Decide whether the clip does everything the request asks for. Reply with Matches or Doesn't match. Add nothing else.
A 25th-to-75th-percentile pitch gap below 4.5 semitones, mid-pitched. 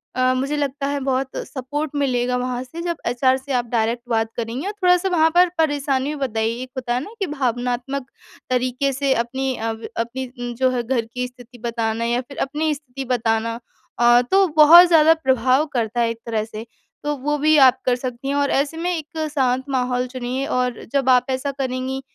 Doesn't match